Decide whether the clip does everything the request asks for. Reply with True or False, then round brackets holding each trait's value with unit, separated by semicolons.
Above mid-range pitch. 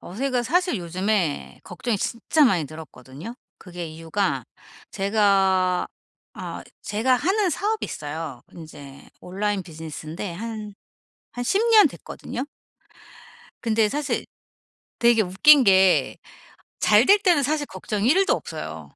True (205 Hz)